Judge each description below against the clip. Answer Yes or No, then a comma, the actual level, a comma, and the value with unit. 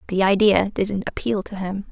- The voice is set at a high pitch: Yes, high, 195 Hz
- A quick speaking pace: No, average, 190 wpm